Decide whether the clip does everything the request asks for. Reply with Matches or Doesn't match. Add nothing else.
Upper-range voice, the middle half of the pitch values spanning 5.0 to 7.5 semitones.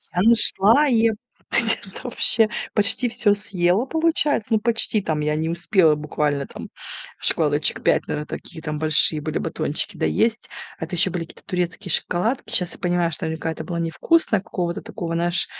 Doesn't match